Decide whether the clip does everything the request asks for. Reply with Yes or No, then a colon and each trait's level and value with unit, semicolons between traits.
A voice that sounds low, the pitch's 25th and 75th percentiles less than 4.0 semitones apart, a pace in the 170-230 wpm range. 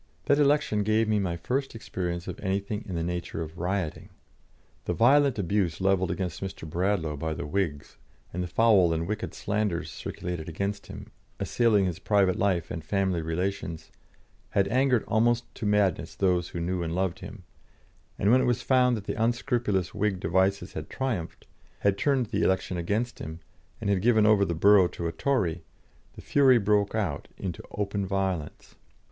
Yes: low, 100 Hz; average, 3.6 semitones; average, 175 wpm